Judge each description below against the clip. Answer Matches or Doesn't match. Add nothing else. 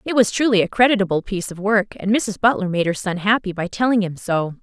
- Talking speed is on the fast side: Matches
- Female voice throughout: Matches